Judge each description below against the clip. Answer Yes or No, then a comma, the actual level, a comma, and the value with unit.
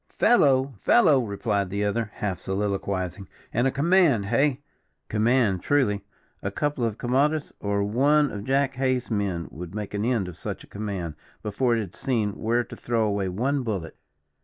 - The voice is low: Yes, low, 110 Hz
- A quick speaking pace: No, average, 170 wpm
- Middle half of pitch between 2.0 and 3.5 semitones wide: No, average, 4.8 semitones